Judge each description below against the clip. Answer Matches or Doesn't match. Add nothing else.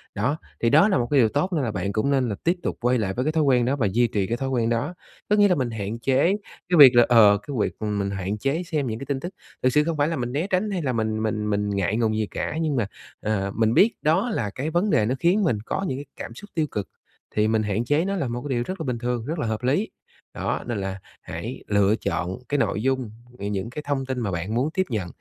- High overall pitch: Doesn't match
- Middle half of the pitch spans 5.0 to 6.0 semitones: Matches